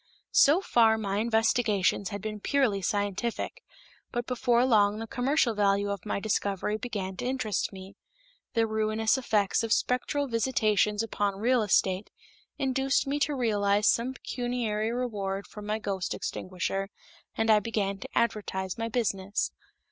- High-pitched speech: Yes, high, 215 Hz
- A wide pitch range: No, average, 3.2 semitones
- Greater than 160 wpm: No, average, 145 wpm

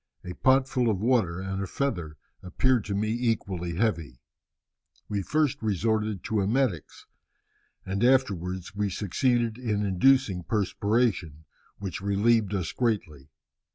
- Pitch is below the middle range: Yes, low, 105 Hz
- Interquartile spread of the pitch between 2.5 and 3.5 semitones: No, average, 4.4 semitones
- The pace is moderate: No, slow, 125 wpm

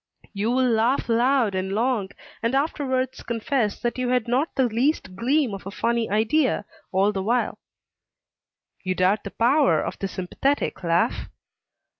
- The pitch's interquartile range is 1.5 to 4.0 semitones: No, average, 4.5 semitones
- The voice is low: No, high, 235 Hz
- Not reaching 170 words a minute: Yes, average, 155 wpm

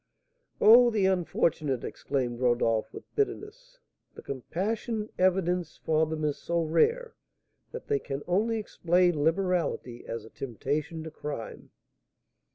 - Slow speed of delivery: Yes, slow, 125 wpm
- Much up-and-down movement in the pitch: Yes, wide, 6.8 semitones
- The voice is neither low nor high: Yes, medium, 170 Hz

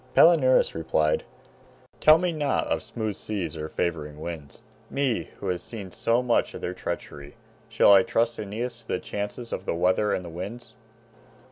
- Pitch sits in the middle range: No, low, 105 Hz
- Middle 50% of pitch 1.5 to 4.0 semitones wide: No, wide, 5.6 semitones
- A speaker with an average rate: Yes, average, 170 wpm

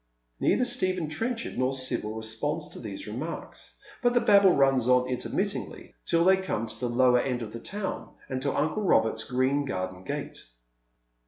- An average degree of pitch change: No, wide, 7.7 semitones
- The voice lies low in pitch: Yes, low, 130 Hz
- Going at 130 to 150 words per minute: No, average, 170 wpm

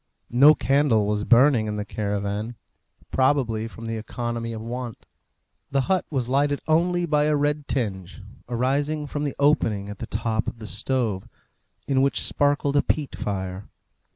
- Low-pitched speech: Yes, low, 125 Hz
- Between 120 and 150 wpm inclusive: No, average, 160 wpm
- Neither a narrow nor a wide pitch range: Yes, average, 4.8 semitones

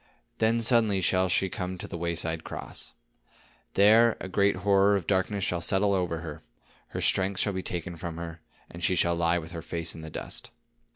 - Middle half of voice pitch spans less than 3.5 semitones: Yes, average, 2.9 semitones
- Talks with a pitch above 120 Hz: No, very low, 90 Hz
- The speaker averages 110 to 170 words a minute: No, average, 195 wpm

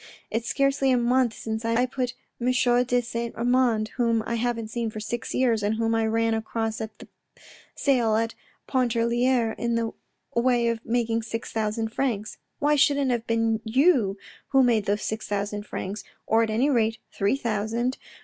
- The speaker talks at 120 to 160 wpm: No, average, 180 wpm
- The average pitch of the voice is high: Yes, high, 230 Hz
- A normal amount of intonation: No, narrow, 1.9 semitones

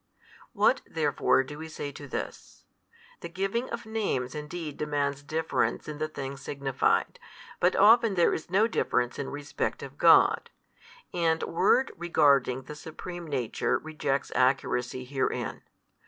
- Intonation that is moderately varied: Yes, average, 4.0 semitones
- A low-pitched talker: No, medium, 150 Hz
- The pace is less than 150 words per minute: Yes, average, 140 wpm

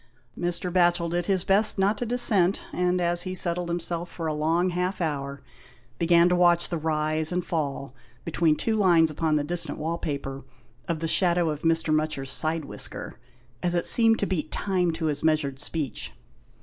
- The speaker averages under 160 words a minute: No, average, 185 wpm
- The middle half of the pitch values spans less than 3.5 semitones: Yes, narrow, 2.5 semitones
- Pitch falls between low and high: Yes, medium, 170 Hz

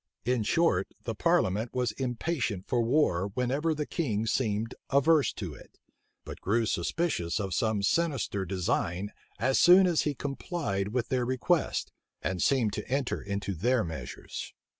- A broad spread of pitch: Yes, wide, 5.8 semitones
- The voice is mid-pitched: No, low, 120 Hz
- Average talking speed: Yes, average, 150 wpm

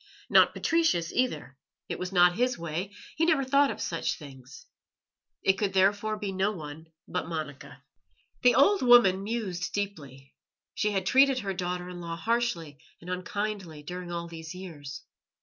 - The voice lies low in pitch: No, medium, 185 Hz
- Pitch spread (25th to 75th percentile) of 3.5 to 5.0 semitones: Yes, average, 4.4 semitones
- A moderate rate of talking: Yes, average, 160 wpm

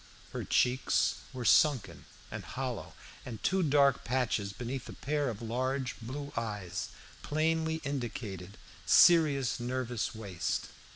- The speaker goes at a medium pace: No, slow, 120 wpm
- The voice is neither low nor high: No, low, 125 Hz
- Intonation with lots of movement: No, average, 4.2 semitones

